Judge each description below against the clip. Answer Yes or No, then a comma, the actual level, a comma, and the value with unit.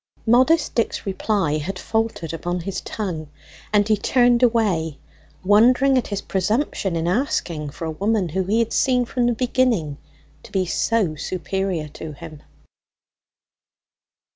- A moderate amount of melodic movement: No, wide, 5.7 semitones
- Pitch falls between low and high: No, high, 195 Hz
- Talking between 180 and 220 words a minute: No, average, 140 wpm